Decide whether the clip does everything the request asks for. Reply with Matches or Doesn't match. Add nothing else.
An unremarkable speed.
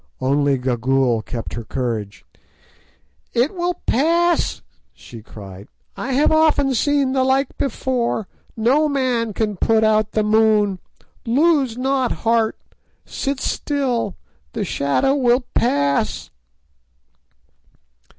Doesn't match